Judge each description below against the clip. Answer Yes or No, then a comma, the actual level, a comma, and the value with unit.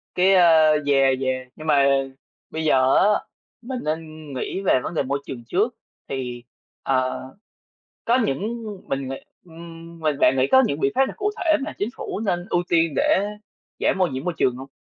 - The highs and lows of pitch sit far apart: Yes, wide, 5.7 semitones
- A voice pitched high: No, medium, 160 Hz